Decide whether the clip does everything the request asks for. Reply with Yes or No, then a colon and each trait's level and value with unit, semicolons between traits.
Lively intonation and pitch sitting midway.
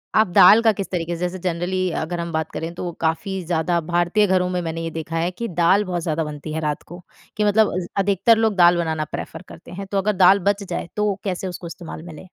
No: average, 2.8 semitones; medium, 180 Hz